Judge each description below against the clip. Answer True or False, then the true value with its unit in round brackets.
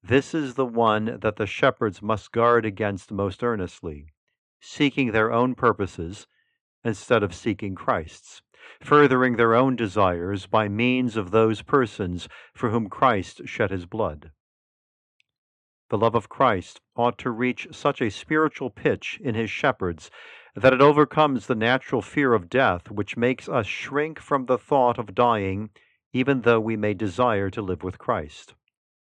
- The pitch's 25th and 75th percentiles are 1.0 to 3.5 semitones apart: False (4.2 semitones)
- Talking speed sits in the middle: True (155 wpm)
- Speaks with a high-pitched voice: False (115 Hz)